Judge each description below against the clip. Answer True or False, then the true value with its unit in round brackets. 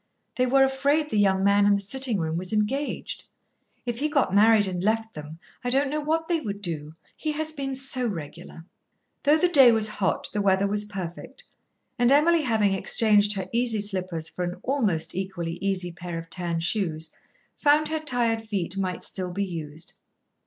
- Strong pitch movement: True (6.6 semitones)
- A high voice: True (205 Hz)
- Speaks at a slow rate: False (190 wpm)